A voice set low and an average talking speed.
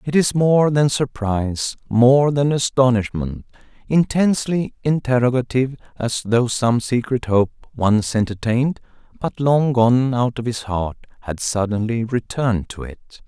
No: low, 125 Hz; slow, 120 wpm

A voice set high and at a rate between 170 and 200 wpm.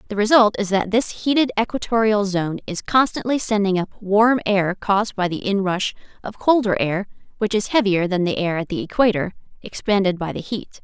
Yes: high, 205 Hz; average, 190 wpm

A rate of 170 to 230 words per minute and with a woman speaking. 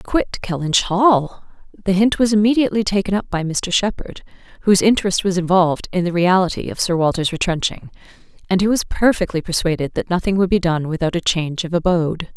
Yes: average, 185 wpm; female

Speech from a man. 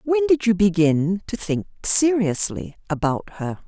No: female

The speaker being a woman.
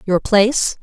Yes: female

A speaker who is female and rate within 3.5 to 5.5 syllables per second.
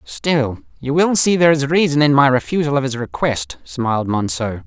No: male; 5.0 syllables/s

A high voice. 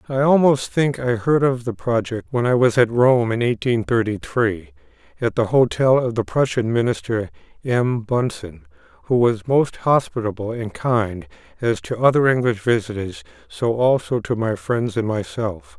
No: low, 120 Hz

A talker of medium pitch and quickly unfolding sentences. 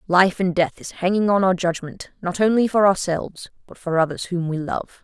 Yes: medium, 180 Hz; fast, 215 wpm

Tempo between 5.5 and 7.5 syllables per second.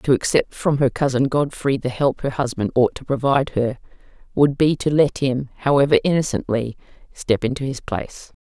No: 5.3 syllables/s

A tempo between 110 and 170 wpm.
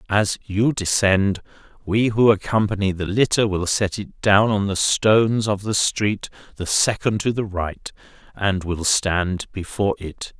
Yes: average, 160 wpm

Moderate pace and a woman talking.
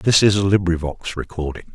No: average, 170 wpm; male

